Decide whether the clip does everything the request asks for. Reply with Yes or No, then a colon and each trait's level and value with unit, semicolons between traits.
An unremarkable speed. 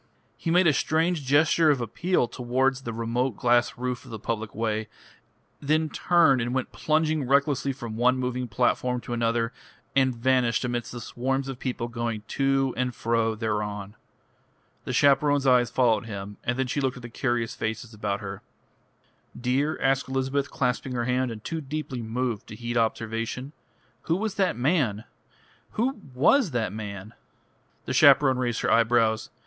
Yes: average, 165 wpm